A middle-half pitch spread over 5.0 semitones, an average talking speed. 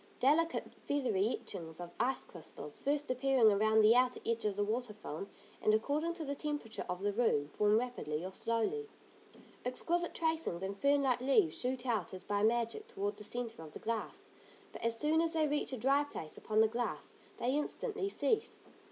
Yes: wide, 5.6 semitones; average, 190 wpm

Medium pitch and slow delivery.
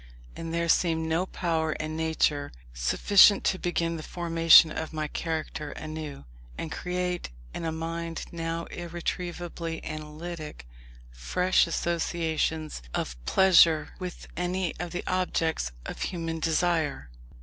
Yes: medium, 165 Hz; slow, 125 wpm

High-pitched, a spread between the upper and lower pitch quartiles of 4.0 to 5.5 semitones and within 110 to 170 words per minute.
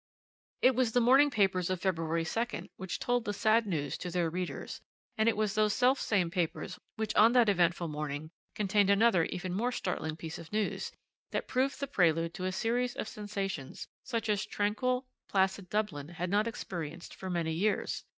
No: high, 195 Hz; average, 4.6 semitones; average, 180 wpm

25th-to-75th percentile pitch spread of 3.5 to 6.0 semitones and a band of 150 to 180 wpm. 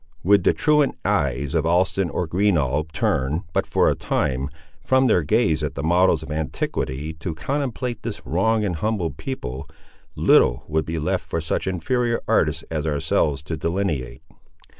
Yes: average, 5.2 semitones; average, 160 wpm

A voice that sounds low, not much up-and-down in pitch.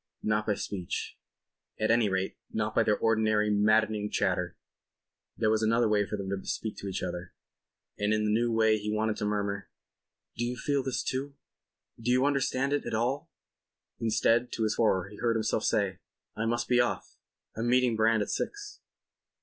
Yes: low, 110 Hz; narrow, 2.3 semitones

